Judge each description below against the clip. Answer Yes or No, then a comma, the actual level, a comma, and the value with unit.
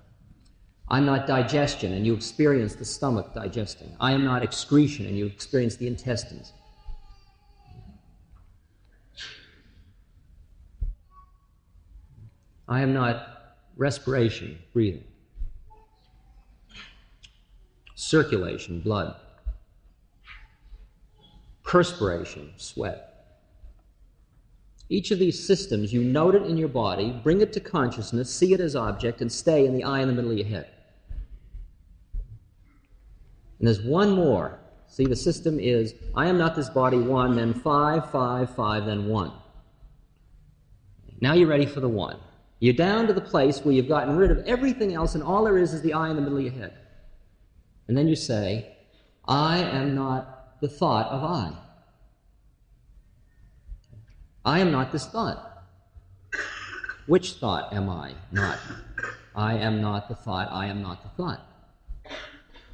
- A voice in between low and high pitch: No, low, 115 Hz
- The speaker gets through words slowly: Yes, slow, 130 wpm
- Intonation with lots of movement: Yes, wide, 6.4 semitones